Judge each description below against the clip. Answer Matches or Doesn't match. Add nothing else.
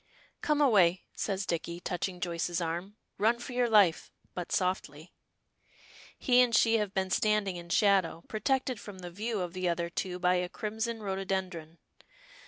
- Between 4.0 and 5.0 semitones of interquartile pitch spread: Doesn't match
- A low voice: Doesn't match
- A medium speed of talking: Matches